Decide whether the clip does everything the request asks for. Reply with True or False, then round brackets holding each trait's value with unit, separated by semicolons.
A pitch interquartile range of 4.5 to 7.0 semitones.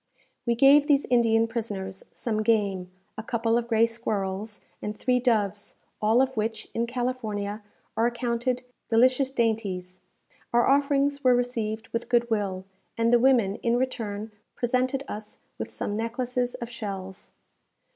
False (2.8 semitones)